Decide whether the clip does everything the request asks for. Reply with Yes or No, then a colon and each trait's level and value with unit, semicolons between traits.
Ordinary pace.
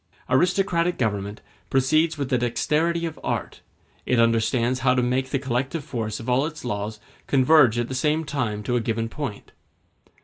Yes: average, 170 wpm